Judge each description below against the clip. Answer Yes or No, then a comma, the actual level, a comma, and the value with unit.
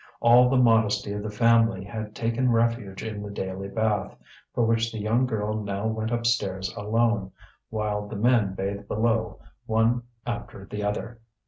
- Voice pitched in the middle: No, low, 110 Hz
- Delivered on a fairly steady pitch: Yes, narrow, 2.1 semitones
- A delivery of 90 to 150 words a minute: No, average, 160 wpm